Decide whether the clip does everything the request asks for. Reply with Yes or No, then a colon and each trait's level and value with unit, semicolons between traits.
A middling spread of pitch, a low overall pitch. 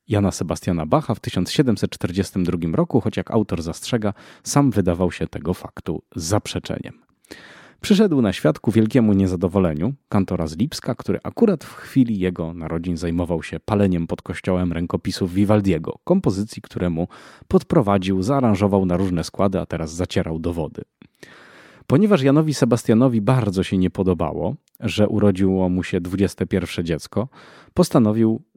Yes: average, 3.9 semitones; very low, 95 Hz